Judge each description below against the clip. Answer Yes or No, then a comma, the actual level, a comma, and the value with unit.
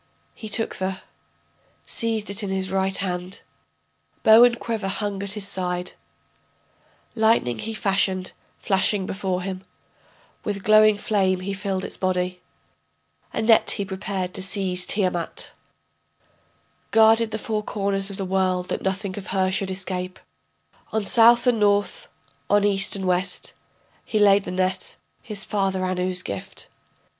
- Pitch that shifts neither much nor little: No, narrow, 2.1 semitones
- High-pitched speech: Yes, high, 195 Hz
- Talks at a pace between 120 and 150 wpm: Yes, average, 145 wpm